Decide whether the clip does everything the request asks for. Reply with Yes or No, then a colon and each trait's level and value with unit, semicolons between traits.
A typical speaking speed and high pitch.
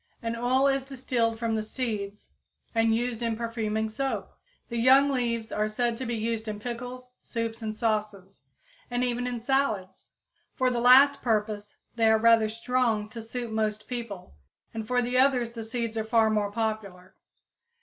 Yes: average, 170 wpm; high, 230 Hz